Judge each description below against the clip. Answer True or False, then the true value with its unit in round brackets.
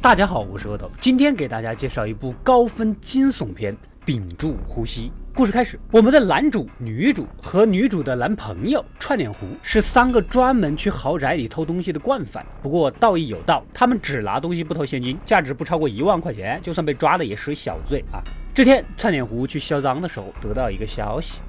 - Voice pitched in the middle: True (160 Hz)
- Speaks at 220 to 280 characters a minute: False (315 characters per minute)